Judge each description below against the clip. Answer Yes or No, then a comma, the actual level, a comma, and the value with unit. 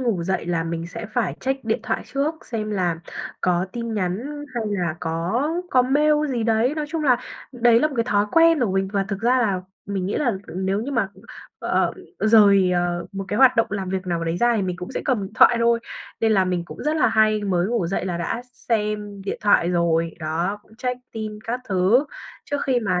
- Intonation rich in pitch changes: No, average, 4.8 semitones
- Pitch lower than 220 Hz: Yes, high, 210 Hz